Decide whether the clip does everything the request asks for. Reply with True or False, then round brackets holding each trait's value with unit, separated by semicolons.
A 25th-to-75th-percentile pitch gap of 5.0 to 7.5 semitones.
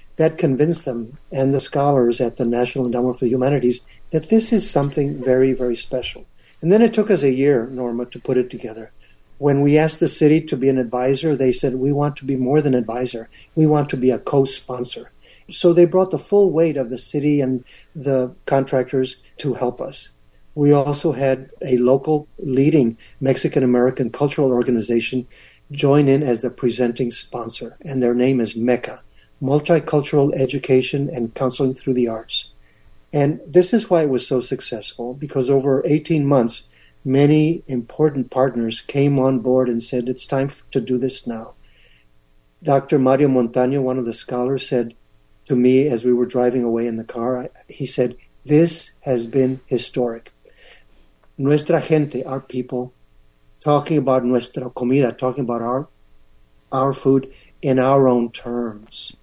False (2.6 semitones)